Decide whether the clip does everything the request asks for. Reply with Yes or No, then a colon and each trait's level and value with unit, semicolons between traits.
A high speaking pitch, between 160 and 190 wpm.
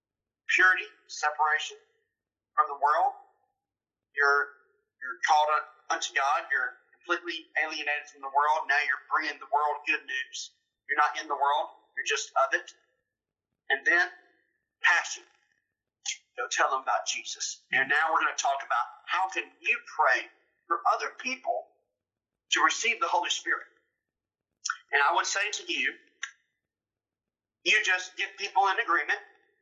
No: very high, 345 Hz; average, 145 wpm